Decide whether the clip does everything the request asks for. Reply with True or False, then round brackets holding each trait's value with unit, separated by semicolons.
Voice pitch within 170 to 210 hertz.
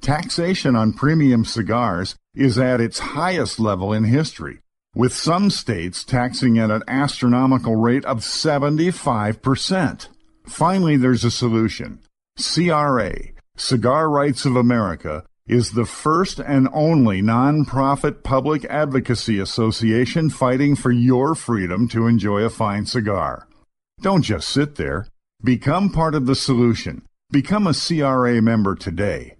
False (125 Hz)